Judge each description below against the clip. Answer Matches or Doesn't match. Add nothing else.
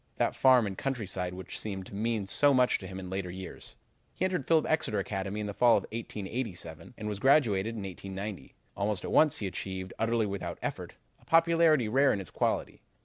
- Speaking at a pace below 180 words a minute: Doesn't match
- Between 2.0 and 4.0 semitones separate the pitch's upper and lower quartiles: Doesn't match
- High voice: Doesn't match